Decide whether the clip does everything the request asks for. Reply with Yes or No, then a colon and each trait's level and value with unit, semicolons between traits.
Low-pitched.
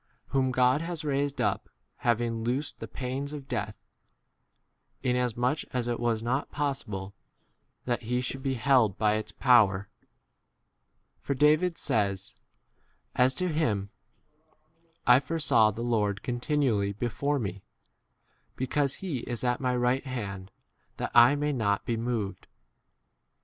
Yes: low, 125 Hz